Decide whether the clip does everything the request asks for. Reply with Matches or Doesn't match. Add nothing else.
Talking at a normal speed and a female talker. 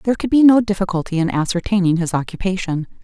Matches